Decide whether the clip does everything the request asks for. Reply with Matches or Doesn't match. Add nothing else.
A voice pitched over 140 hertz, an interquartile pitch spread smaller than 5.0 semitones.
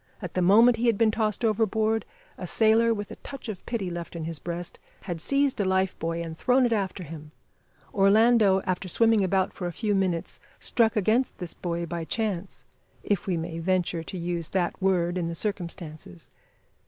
Matches